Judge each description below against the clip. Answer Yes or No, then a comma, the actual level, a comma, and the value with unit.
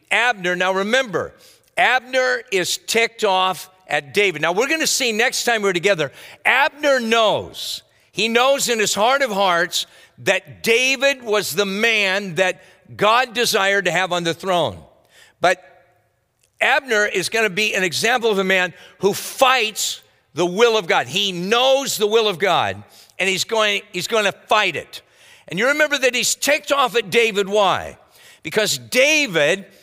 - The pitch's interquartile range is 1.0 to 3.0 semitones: No, average, 4.7 semitones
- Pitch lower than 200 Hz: No, high, 210 Hz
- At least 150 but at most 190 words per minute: Yes, average, 165 wpm